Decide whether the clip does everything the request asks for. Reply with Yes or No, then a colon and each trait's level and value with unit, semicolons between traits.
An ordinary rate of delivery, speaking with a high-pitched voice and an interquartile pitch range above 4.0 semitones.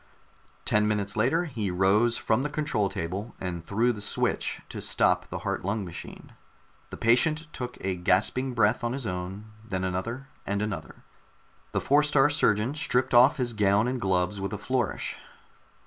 No: average, 170 wpm; low, 110 Hz; average, 4.6 semitones